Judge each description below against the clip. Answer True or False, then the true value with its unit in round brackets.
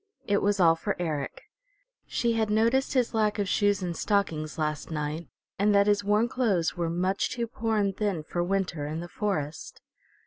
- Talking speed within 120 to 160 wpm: False (185 wpm)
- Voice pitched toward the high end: True (200 Hz)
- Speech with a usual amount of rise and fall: True (4.2 semitones)